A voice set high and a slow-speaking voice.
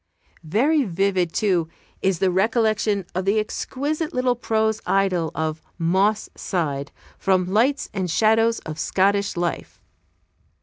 Yes: high, 195 Hz; slow, 125 wpm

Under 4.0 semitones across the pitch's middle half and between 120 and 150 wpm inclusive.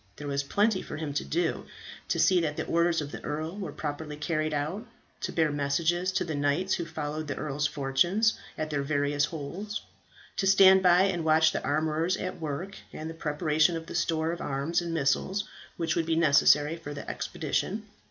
No: average, 3.0 semitones; average, 200 wpm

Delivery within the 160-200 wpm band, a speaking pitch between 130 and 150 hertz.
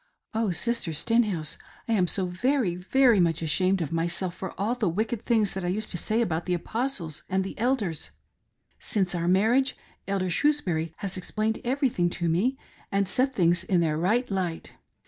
No: average, 185 wpm; high, 190 Hz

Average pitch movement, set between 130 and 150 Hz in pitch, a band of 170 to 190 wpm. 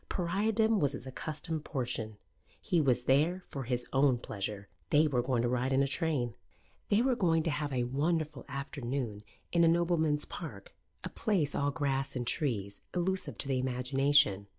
Yes: average, 4.5 semitones; medium, 140 Hz; average, 175 wpm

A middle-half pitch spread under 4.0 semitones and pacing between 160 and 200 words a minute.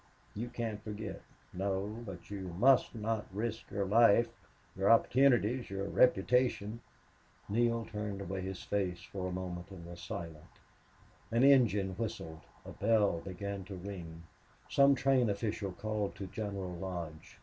No: average, 3.4 semitones; average, 140 wpm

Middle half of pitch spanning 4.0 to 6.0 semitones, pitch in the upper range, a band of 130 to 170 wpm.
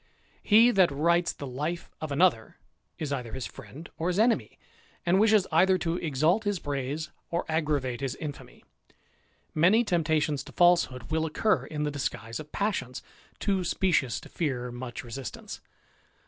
No: average, 4.8 semitones; medium, 155 Hz; average, 160 wpm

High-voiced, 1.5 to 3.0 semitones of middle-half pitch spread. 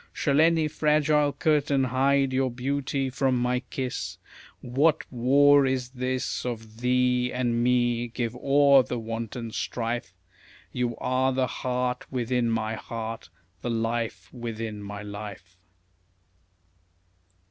No: low, 125 Hz; narrow, 2.5 semitones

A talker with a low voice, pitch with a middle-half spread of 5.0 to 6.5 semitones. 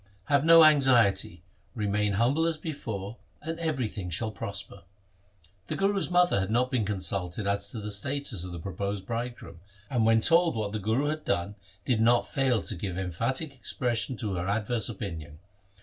Yes: low, 110 Hz; average, 5.3 semitones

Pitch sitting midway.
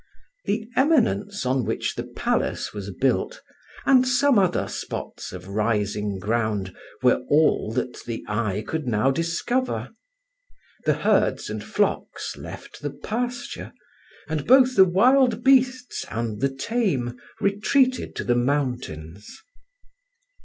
Yes: medium, 145 Hz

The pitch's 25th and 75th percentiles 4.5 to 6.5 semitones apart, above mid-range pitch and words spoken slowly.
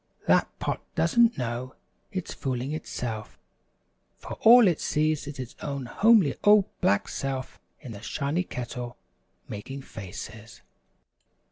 No: average, 5.3 semitones; low, 135 Hz; slow, 125 wpm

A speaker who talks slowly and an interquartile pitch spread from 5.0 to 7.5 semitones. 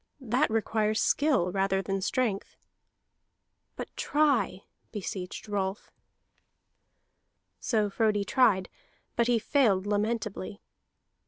No: slow, 90 wpm; average, 3.3 semitones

